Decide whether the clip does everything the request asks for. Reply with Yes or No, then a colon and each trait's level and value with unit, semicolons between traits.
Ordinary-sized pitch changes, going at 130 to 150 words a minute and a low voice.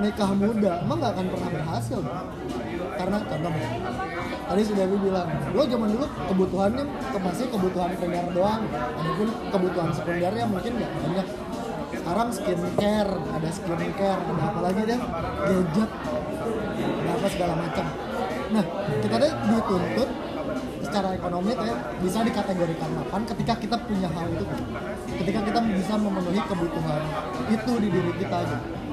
No: average, 3.2 semitones; average, 135 wpm; high, 195 Hz